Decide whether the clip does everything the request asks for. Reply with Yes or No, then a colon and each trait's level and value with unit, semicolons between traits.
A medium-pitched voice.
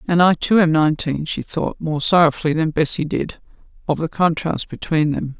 Yes: medium, 160 Hz